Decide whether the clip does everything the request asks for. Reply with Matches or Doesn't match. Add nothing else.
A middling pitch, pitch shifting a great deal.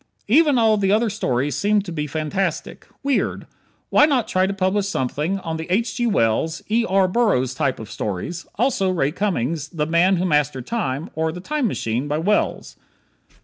Matches